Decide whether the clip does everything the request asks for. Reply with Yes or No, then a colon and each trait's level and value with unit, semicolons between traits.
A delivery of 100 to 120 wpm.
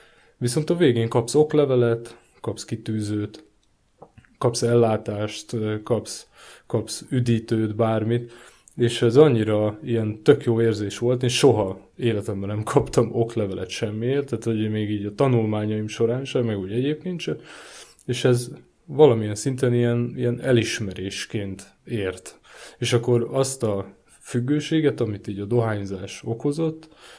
No: average, 130 wpm